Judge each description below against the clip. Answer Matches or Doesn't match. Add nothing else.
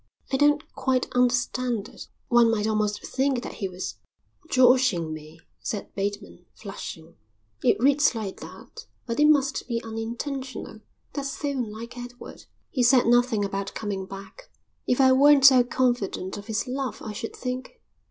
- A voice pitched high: Matches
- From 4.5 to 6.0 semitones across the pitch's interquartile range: Doesn't match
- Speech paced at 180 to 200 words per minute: Doesn't match